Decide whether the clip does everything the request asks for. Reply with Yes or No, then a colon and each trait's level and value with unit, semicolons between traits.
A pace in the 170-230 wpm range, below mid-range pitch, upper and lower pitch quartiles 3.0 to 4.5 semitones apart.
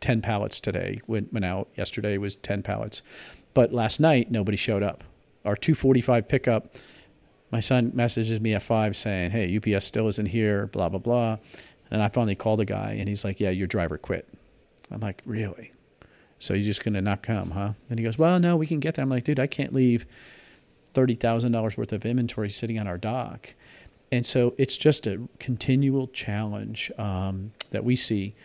Yes: average, 195 wpm; low, 110 Hz; average, 3.3 semitones